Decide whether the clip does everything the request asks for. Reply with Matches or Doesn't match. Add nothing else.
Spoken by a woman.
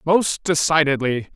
Doesn't match